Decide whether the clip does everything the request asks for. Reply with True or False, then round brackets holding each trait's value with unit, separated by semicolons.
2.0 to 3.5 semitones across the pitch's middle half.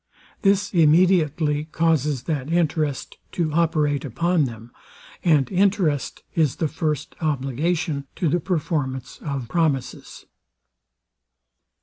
True (3.2 semitones)